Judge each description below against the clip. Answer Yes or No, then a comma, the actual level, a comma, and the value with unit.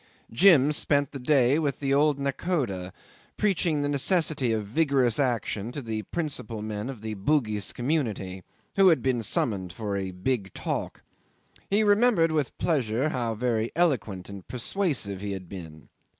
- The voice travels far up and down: Yes, wide, 6.3 semitones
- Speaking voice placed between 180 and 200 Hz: No, low, 125 Hz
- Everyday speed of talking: Yes, average, 155 wpm